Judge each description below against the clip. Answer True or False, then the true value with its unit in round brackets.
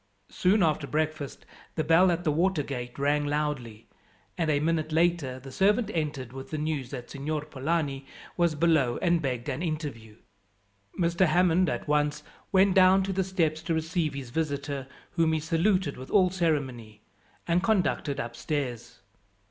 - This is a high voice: False (155 Hz)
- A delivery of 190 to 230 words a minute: False (160 wpm)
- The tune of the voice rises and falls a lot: False (3.7 semitones)